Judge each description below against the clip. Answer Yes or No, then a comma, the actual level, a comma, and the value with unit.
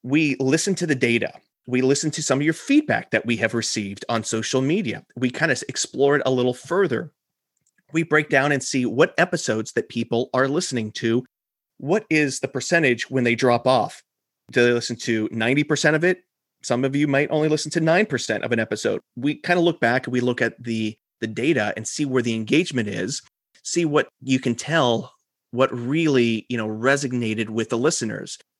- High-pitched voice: No, low, 130 Hz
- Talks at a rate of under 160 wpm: No, fast, 205 wpm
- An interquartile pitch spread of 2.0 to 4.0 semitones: No, average, 4.5 semitones